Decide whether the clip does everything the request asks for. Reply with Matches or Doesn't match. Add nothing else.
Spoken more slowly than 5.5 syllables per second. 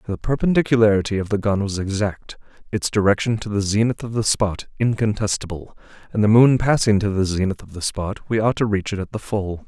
Doesn't match